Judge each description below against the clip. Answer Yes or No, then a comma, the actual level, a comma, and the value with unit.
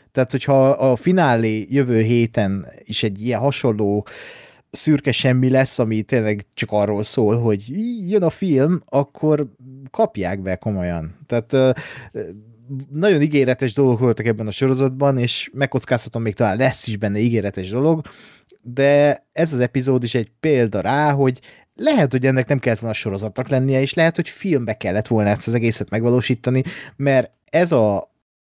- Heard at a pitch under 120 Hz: No, low, 130 Hz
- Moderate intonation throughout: Yes, average, 4.0 semitones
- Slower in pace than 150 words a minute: No, fast, 155 wpm